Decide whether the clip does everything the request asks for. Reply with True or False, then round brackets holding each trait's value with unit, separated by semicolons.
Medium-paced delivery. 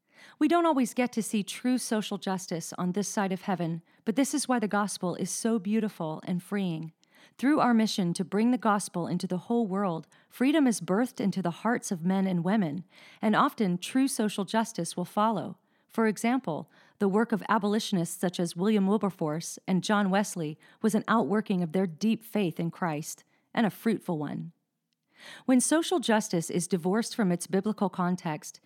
True (185 wpm)